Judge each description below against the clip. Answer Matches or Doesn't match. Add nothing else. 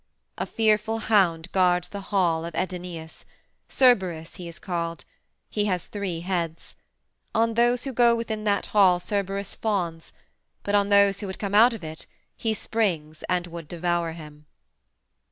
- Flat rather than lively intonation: Doesn't match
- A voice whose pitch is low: Doesn't match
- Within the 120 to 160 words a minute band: Matches